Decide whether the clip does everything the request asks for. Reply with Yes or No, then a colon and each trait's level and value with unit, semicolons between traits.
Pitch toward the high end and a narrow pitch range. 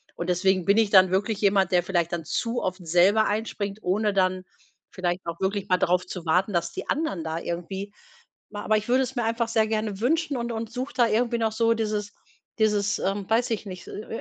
No: high, 205 Hz; average, 3.4 semitones